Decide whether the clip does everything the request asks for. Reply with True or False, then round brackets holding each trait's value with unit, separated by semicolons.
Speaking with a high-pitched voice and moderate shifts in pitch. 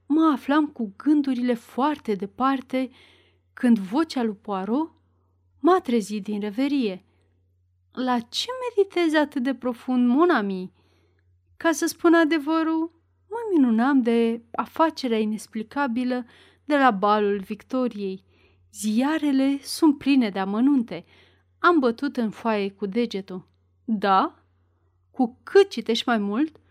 False (235 Hz; 6.8 semitones)